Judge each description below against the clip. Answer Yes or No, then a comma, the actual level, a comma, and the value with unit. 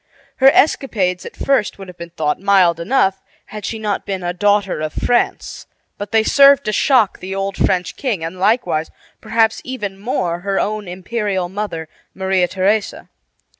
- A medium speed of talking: Yes, average, 170 wpm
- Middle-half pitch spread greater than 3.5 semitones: No, average, 3.1 semitones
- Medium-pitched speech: No, high, 195 Hz